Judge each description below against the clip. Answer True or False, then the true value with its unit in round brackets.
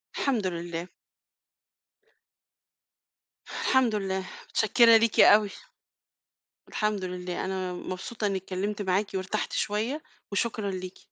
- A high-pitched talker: True (195 Hz)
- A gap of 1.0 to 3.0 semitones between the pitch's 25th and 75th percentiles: True (2.6 semitones)